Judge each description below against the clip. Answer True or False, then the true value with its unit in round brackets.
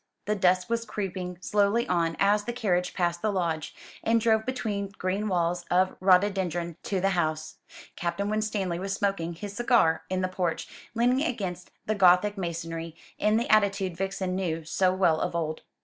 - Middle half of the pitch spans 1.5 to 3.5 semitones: True (3.1 semitones)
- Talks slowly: False (170 wpm)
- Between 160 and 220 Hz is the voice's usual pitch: True (185 Hz)